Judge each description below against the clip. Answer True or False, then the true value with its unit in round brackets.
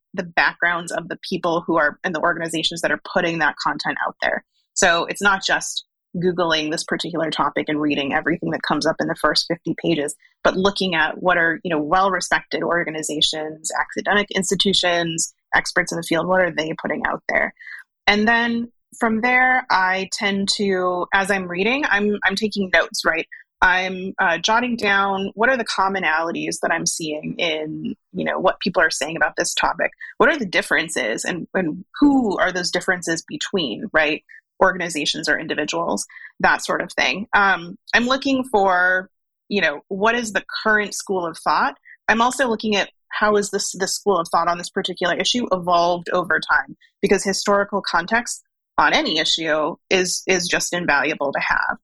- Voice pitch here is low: False (185 Hz)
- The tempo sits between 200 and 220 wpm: False (180 wpm)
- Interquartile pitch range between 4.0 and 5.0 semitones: False (3.4 semitones)